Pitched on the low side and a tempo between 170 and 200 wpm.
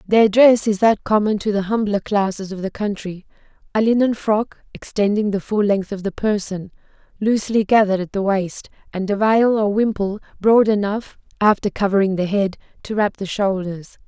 No: high, 205 Hz; average, 175 wpm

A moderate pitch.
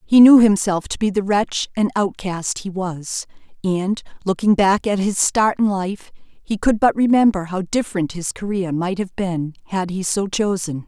No: high, 195 Hz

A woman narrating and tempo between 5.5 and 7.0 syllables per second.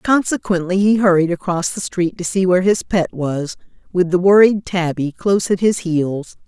No: female; 4.9 syllables/s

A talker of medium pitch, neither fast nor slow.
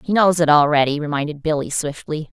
Yes: medium, 155 Hz; average, 175 wpm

